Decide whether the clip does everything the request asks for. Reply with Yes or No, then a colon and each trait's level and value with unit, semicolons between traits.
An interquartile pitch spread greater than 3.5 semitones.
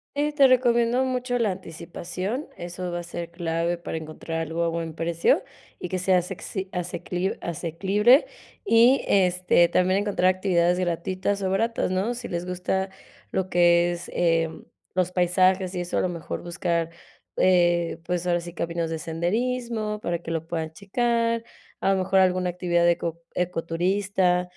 No: narrow, 2.5 semitones